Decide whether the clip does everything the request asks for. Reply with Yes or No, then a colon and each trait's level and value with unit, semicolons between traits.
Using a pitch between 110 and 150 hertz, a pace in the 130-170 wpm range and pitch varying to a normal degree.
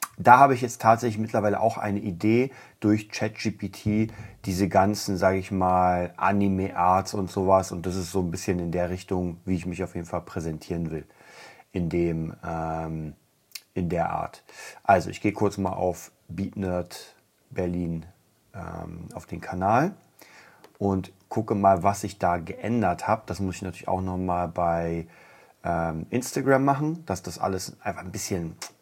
No: very low, 95 Hz; average, 160 wpm; average, 3.1 semitones